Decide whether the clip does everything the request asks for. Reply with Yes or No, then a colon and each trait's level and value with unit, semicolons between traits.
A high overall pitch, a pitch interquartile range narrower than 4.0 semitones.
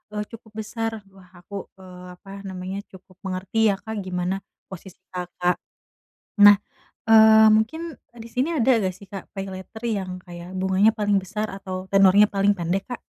Yes: high, 195 Hz; average, 2.9 semitones